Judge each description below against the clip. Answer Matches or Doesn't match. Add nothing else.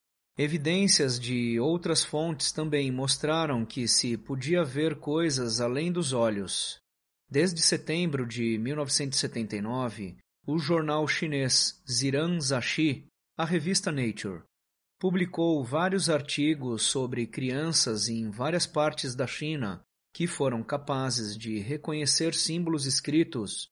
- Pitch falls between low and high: Matches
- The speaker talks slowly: Matches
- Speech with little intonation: Doesn't match